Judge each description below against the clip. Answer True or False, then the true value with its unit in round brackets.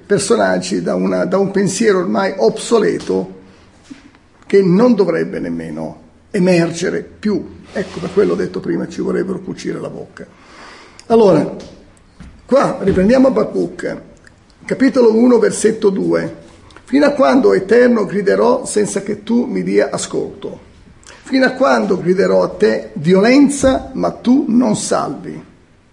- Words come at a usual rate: True (125 wpm)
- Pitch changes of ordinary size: False (6.3 semitones)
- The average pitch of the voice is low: False (205 Hz)